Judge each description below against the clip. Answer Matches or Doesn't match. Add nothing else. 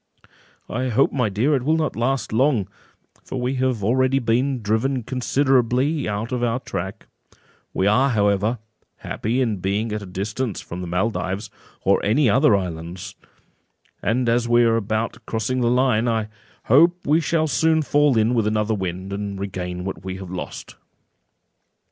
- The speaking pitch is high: Doesn't match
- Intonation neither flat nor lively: Matches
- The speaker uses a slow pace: Doesn't match